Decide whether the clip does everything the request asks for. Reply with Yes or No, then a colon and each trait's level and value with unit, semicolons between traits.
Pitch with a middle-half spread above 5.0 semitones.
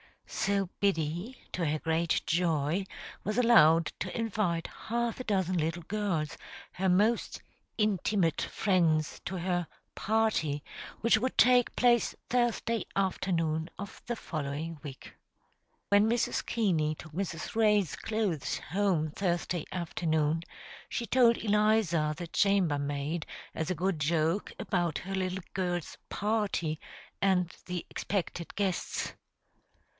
No: average, 4.6 semitones